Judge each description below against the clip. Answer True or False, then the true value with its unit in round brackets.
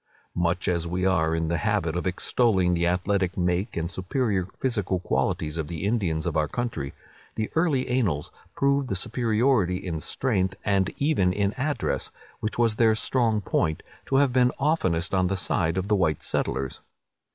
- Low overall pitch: True (95 Hz)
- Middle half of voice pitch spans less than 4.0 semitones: False (5.4 semitones)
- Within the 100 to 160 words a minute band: False (175 wpm)